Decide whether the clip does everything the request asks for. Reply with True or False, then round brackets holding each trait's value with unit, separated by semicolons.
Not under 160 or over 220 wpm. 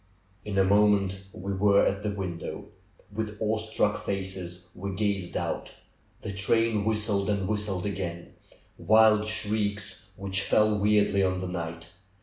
False (145 wpm)